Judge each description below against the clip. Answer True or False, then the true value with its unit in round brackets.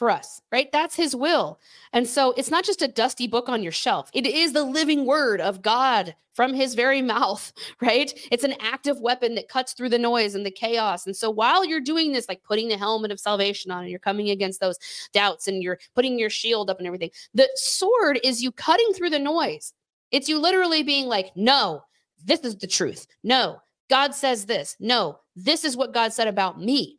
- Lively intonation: True (5.7 semitones)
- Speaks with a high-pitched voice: True (245 Hz)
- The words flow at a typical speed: False (220 wpm)